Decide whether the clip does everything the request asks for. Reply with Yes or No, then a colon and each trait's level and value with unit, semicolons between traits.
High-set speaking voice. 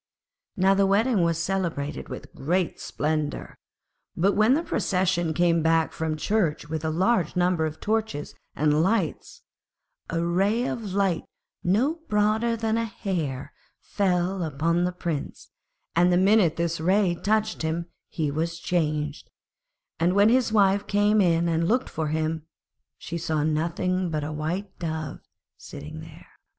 No: medium, 175 Hz